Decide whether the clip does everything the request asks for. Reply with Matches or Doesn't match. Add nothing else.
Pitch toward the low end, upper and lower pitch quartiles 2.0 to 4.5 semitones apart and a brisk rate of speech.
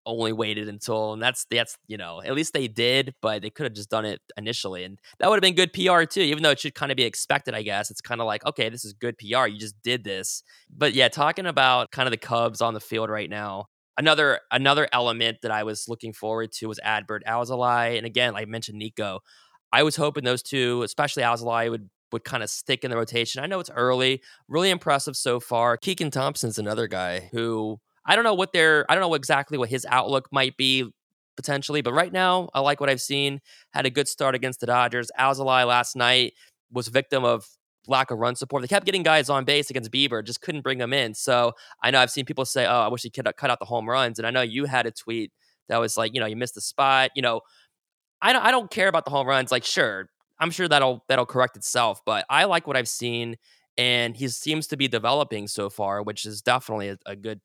Matches